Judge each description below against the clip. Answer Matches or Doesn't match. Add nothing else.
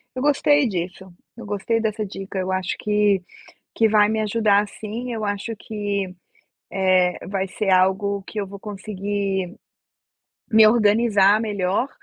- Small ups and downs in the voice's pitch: Matches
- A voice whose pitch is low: Doesn't match